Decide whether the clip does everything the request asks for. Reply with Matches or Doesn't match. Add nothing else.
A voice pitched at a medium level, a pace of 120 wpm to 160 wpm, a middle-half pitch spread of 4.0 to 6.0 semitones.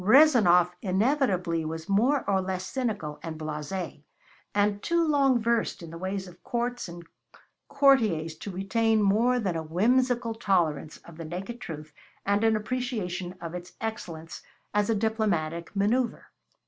Doesn't match